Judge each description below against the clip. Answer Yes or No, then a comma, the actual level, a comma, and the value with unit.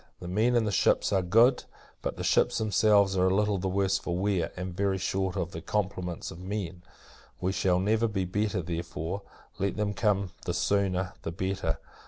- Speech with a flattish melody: Yes, narrow, 2.2 semitones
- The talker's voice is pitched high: No, very low, 95 Hz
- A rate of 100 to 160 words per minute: No, average, 195 wpm